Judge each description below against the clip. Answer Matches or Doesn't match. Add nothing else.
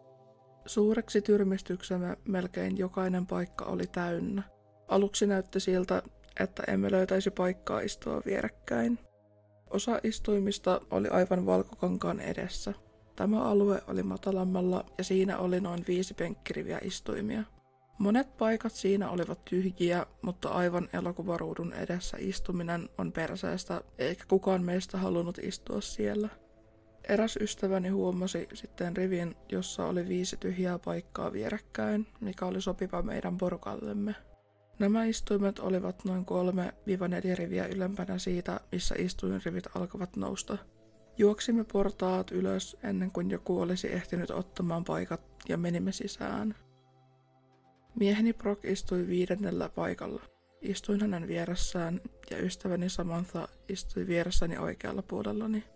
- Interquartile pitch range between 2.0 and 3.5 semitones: Matches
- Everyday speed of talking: Matches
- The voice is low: Doesn't match